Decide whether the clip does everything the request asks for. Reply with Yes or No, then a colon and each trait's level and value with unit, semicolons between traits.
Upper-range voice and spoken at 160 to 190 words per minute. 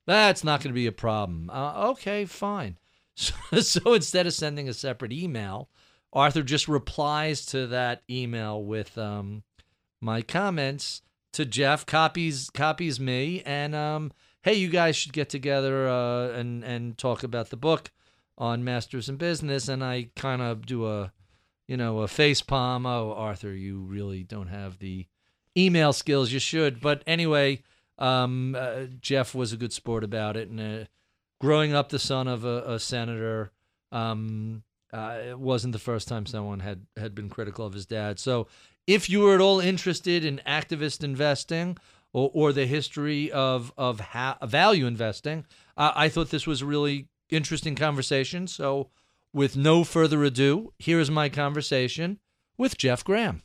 No: low, 135 Hz; average, 165 wpm